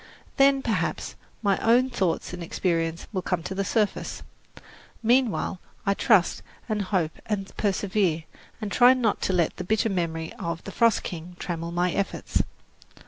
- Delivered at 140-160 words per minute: Yes, average, 155 wpm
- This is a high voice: Yes, high, 195 Hz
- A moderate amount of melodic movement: Yes, average, 4.2 semitones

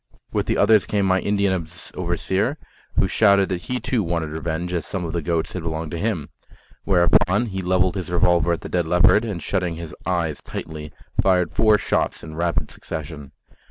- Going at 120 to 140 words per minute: No, average, 190 wpm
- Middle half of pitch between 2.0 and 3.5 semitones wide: Yes, average, 2.8 semitones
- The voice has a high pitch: No, very low, 90 Hz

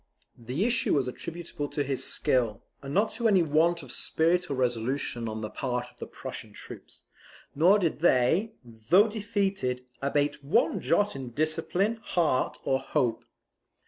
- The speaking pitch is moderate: Yes, medium, 145 Hz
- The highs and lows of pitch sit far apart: Yes, wide, 6.4 semitones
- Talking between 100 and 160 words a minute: Yes, average, 155 wpm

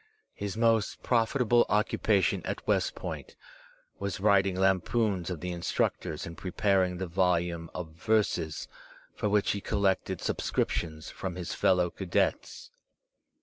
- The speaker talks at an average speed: No, slow, 125 wpm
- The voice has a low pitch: Yes, very low, 95 Hz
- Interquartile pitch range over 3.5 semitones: No, average, 2.9 semitones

